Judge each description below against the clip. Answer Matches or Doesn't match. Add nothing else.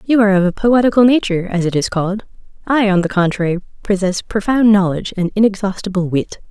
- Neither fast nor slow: Matches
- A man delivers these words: Doesn't match